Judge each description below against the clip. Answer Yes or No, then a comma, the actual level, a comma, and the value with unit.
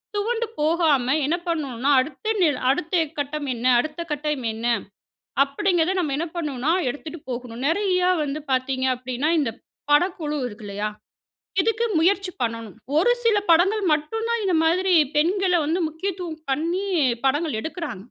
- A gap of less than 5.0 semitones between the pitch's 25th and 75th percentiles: No, average, 5.3 semitones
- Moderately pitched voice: No, very high, 310 Hz